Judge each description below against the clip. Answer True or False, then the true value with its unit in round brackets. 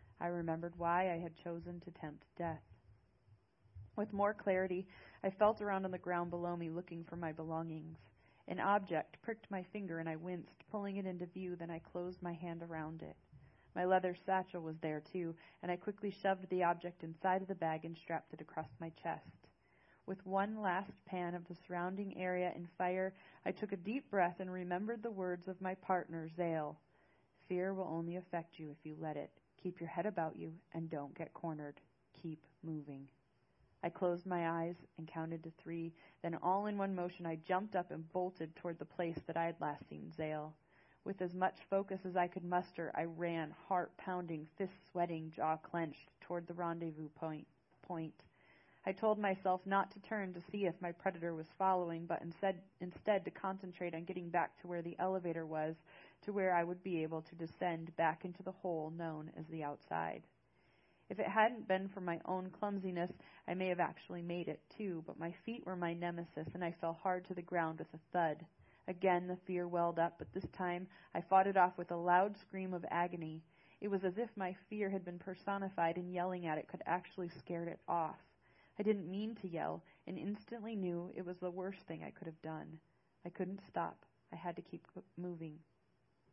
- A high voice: False (175 Hz)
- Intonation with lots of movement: False (2.4 semitones)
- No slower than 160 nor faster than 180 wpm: False (200 wpm)